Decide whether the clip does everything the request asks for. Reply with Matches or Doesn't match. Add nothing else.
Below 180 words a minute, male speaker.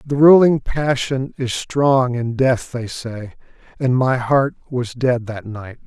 Matches